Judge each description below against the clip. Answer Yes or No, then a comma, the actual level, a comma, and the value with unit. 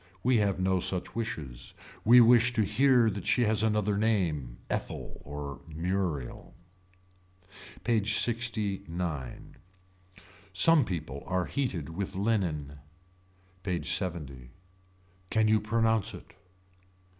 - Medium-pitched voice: No, very low, 95 Hz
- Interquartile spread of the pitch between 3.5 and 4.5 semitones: No, wide, 5.6 semitones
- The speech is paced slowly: Yes, slow, 110 wpm